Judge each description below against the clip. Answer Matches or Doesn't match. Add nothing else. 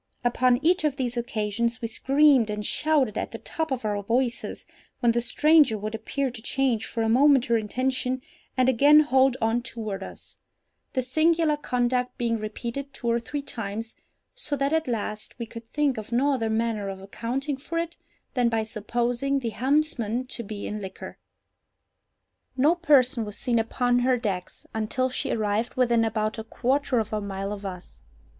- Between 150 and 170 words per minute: Doesn't match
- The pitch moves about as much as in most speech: Matches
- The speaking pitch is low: Doesn't match